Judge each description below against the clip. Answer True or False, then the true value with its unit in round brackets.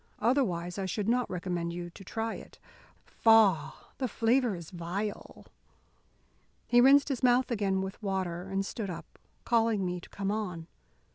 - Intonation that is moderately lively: True (4.3 semitones)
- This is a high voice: True (195 Hz)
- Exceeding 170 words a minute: False (155 wpm)